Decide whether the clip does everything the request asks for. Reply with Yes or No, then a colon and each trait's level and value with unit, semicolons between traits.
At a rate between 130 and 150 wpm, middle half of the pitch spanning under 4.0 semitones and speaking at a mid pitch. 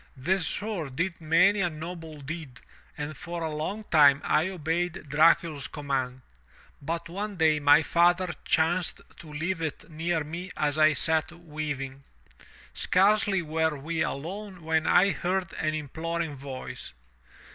Yes: average, 140 wpm; average, 2.7 semitones; medium, 160 Hz